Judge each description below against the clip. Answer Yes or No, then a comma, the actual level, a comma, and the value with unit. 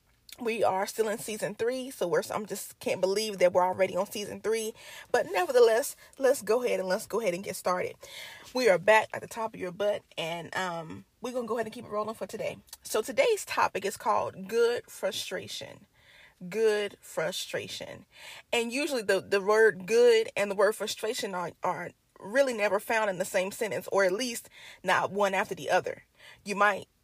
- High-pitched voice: Yes, high, 215 Hz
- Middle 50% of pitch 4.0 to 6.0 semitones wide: Yes, average, 4.3 semitones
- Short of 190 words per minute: No, average, 195 wpm